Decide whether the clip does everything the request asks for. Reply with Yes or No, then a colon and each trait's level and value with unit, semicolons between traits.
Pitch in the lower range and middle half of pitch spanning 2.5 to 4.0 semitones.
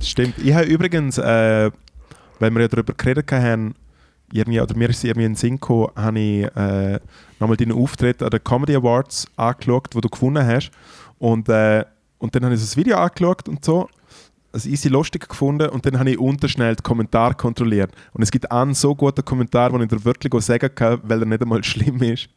Yes: low, 120 Hz; average, 3.3 semitones